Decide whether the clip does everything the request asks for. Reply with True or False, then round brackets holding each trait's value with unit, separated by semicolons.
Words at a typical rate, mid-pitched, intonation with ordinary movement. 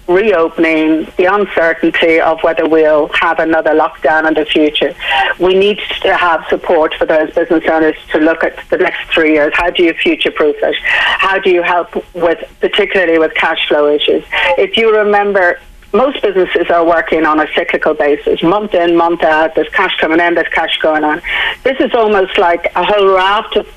True (190 wpm; 170 Hz; 3.3 semitones)